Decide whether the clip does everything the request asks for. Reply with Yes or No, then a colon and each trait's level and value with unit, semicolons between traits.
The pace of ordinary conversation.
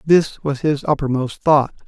Yes: average, 160 wpm